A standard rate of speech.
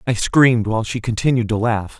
No: fast, 210 wpm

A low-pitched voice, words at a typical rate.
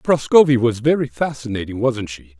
Yes: low, 120 Hz; average, 150 wpm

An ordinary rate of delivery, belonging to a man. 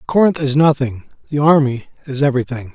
Yes: average, 155 wpm; male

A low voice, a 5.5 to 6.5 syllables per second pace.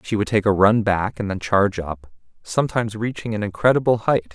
Yes: low, 105 Hz; 5.9 syllables/s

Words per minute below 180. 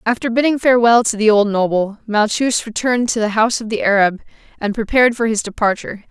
No: average, 195 wpm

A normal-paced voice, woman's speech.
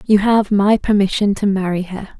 Yes: average, 190 wpm; female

